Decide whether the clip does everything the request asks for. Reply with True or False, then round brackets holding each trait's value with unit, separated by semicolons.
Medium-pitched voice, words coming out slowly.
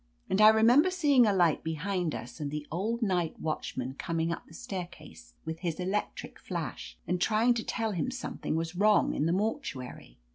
False (180 Hz; 190 wpm)